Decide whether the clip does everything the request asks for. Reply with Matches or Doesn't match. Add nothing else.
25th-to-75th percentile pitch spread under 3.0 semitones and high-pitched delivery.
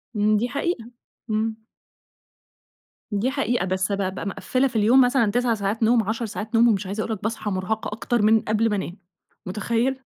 Matches